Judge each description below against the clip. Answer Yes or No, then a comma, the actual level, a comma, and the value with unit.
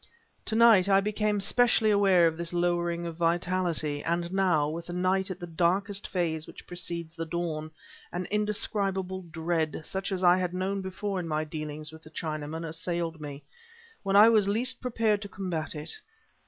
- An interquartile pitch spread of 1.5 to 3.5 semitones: Yes, average, 3.2 semitones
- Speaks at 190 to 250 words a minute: No, average, 180 wpm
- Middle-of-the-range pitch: Yes, medium, 175 Hz